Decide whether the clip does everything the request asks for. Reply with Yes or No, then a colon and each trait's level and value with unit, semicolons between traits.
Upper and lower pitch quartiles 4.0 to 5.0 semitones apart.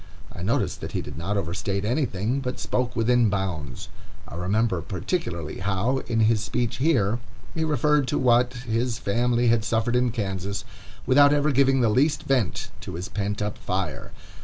Yes: average, 4.4 semitones